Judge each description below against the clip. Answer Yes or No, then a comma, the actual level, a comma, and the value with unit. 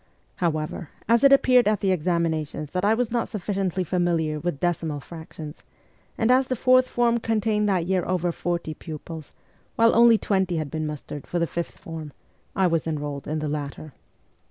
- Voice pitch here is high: No, medium, 175 Hz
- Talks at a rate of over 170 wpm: Yes, average, 180 wpm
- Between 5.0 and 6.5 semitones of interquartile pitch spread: Yes, wide, 5.4 semitones